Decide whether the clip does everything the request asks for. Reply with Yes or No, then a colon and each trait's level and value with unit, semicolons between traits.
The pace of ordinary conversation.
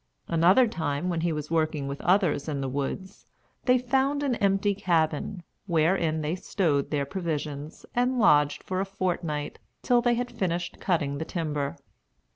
Yes: average, 160 wpm